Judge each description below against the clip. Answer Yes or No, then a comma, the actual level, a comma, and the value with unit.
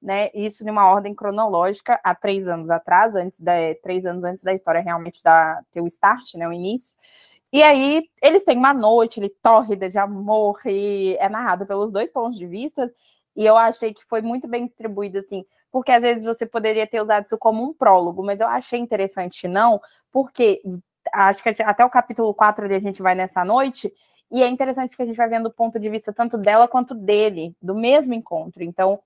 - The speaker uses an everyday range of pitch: Yes, average, 3.7 semitones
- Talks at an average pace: No, fast, 200 wpm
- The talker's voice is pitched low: No, high, 215 Hz